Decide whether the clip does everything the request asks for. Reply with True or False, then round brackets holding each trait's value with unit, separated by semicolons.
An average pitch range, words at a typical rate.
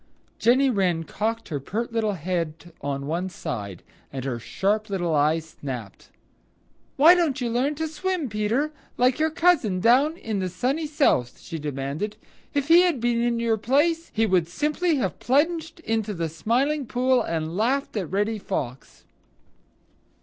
False (8.8 semitones; 160 wpm)